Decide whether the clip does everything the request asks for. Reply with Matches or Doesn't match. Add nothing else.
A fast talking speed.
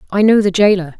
Matches